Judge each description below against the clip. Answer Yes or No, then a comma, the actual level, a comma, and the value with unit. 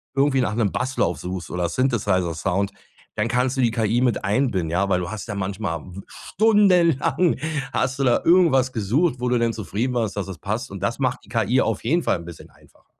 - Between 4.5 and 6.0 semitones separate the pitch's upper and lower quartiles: Yes, average, 5.1 semitones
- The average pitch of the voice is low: Yes, low, 115 Hz